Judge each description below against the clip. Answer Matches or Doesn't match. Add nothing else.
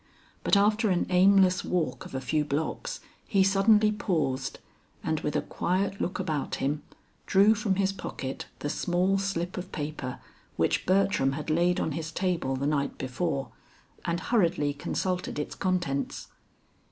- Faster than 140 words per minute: Matches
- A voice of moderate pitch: Matches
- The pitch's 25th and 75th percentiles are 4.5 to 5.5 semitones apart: Matches